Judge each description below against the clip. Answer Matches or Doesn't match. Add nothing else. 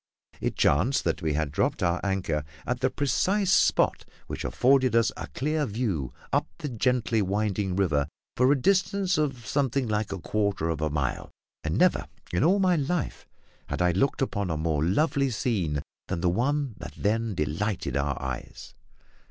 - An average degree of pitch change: Doesn't match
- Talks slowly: Doesn't match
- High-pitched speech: Doesn't match